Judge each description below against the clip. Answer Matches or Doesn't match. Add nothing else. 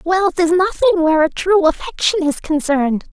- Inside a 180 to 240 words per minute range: Doesn't match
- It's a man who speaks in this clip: Doesn't match